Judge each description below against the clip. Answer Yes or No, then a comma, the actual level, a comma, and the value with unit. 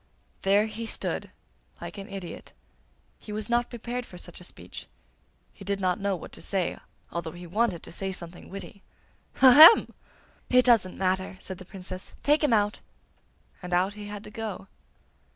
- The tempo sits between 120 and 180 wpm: Yes, average, 170 wpm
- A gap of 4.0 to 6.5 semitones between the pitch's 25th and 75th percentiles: No, average, 3.3 semitones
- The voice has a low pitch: No, high, 200 Hz